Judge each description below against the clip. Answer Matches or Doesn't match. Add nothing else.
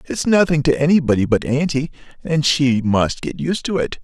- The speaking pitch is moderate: Matches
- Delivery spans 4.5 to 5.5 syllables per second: Matches